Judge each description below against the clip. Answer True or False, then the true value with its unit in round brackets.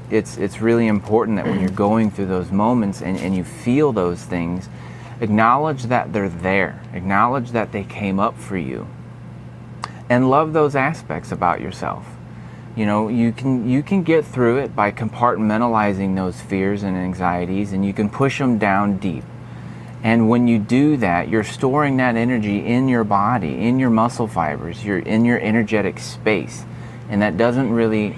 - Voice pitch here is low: True (110 Hz)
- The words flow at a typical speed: True (175 wpm)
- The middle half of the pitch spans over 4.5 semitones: False (3.7 semitones)